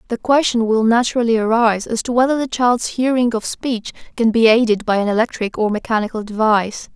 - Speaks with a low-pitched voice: No, high, 230 Hz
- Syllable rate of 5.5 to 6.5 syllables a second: Yes, 5.8 syllables/s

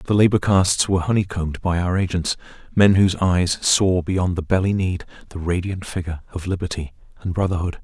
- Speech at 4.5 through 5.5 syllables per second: No, 5.8 syllables/s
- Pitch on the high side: No, very low, 90 Hz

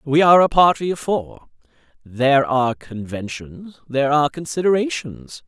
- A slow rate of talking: Yes, slow, 130 wpm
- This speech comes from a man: Yes, male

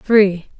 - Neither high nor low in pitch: No, high, 200 Hz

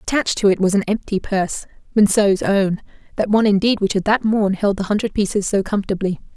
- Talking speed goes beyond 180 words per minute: Yes, average, 200 wpm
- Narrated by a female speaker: Yes, female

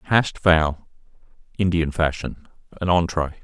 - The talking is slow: Yes, slow, 105 wpm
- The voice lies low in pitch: Yes, very low, 85 Hz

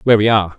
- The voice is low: Yes, low, 105 Hz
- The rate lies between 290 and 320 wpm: Yes, fast, 305 wpm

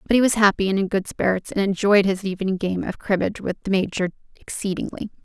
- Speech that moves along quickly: Yes, fast, 220 wpm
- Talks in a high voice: Yes, high, 195 Hz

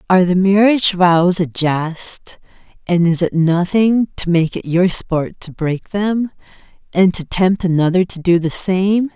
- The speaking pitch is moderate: Yes, medium, 180 Hz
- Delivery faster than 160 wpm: Yes, average, 170 wpm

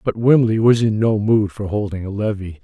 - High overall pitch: No, low, 105 Hz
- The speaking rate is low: No, fast, 230 wpm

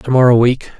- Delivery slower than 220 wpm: No, fast, 225 wpm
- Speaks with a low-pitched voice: Yes, low, 125 Hz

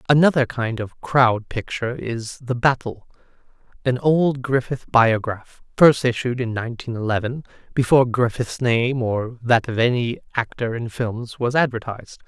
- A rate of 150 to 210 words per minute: No, average, 140 wpm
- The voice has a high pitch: No, low, 120 Hz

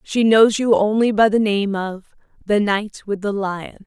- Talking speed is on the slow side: No, average, 200 wpm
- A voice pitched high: Yes, high, 205 Hz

